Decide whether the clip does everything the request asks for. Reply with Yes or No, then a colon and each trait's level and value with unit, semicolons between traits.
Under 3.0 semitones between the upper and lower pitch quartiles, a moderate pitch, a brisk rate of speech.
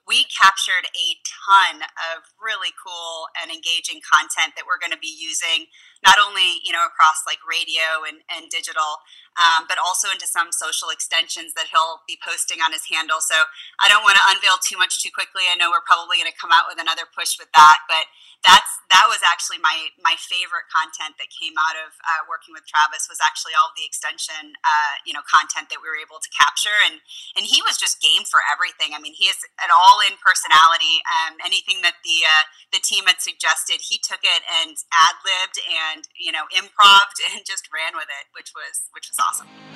Yes: narrow, 2.6 semitones; medium, 165 Hz; fast, 210 wpm